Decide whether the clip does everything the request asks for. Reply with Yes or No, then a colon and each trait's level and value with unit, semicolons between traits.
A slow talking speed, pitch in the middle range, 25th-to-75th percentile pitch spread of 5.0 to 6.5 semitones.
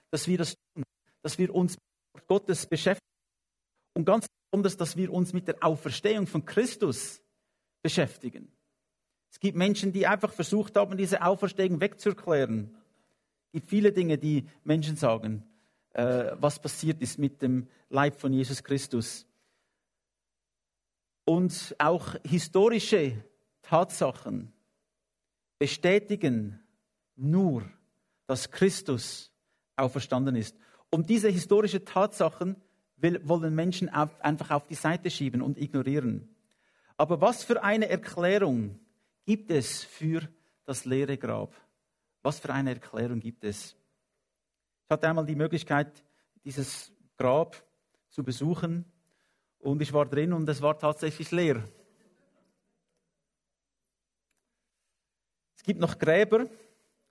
Yes: slow, 120 wpm; medium, 160 Hz; wide, 5.4 semitones